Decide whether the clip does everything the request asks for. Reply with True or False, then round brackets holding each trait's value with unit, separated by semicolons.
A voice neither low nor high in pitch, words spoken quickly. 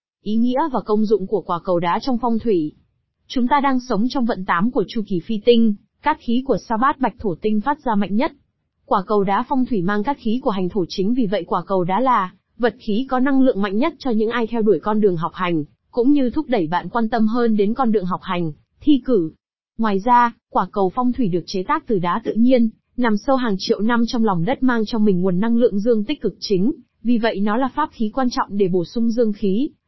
False (225 Hz; 260 wpm)